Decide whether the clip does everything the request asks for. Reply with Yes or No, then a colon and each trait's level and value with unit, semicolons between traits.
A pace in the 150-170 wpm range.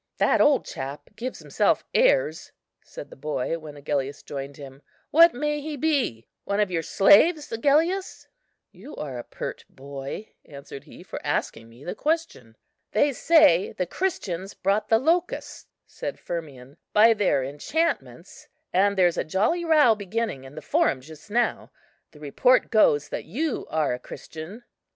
Yes: average, 155 wpm